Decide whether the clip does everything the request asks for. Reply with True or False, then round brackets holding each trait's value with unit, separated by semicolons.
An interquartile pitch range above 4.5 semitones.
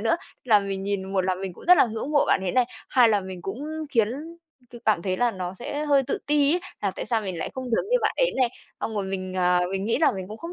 True (5.2 semitones)